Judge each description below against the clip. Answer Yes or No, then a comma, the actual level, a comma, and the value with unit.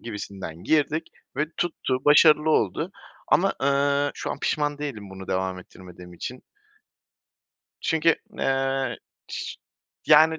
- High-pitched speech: No, medium, 140 Hz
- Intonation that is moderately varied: No, wide, 7.3 semitones